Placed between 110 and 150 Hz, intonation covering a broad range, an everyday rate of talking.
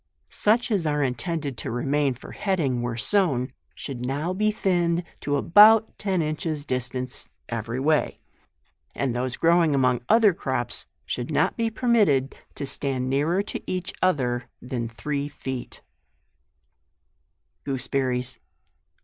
No: medium, 140 Hz; wide, 5.7 semitones; slow, 130 wpm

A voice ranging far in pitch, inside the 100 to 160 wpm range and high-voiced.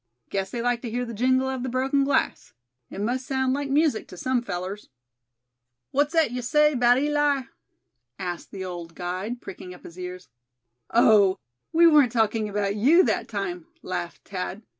No: wide, 5.8 semitones; average, 175 wpm; high, 240 Hz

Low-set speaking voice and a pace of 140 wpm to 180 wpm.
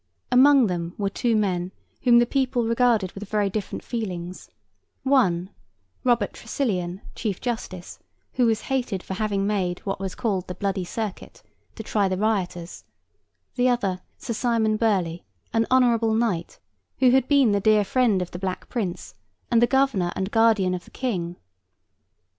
No: high, 215 Hz; average, 160 wpm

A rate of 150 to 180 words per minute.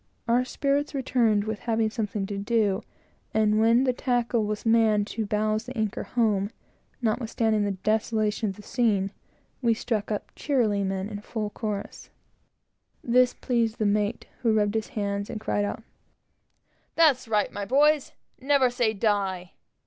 Yes: average, 155 wpm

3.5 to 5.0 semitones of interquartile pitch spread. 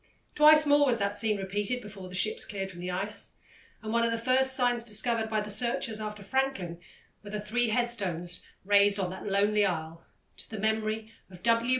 No: average, 3.1 semitones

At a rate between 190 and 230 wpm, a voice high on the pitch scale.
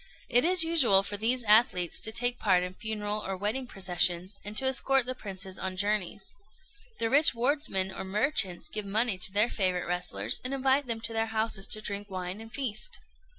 Yes: average, 195 wpm; high, 215 Hz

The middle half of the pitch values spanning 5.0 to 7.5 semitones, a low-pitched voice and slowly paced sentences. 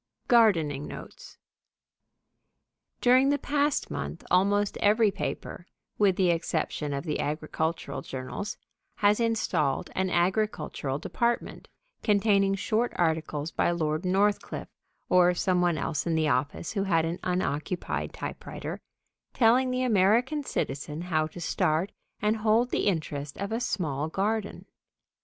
No: wide, 5.4 semitones; medium, 185 Hz; slow, 130 wpm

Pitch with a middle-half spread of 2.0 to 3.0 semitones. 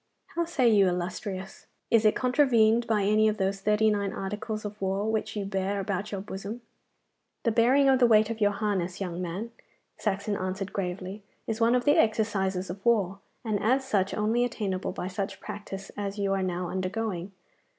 Yes: narrow, 2.5 semitones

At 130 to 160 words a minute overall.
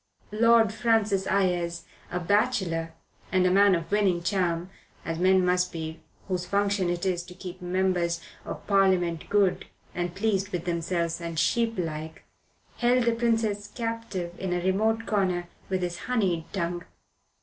Yes: average, 150 wpm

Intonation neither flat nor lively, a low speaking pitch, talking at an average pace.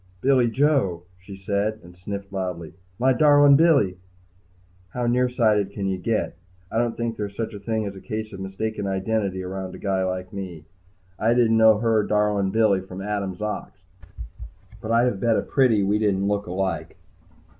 Yes: average, 3.0 semitones; low, 105 Hz; average, 180 wpm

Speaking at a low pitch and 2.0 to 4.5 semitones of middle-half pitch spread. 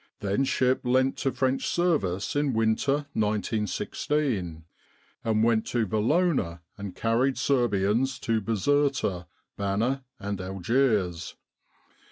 No: low, 115 Hz; average, 5.0 semitones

